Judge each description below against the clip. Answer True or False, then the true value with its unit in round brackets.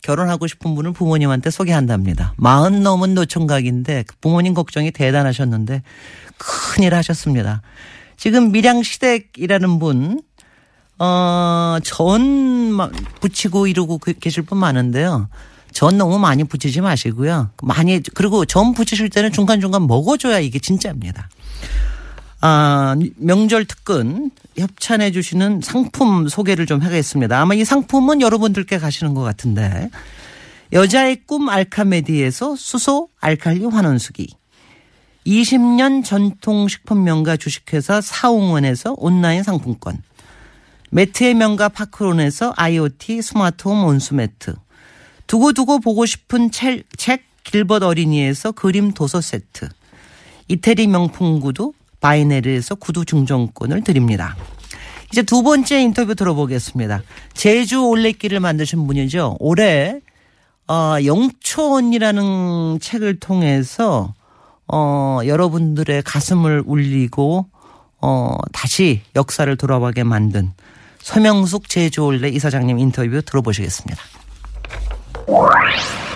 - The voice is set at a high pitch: False (170 Hz)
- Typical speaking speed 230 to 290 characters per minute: True (275 characters per minute)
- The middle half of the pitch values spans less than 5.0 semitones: False (7.0 semitones)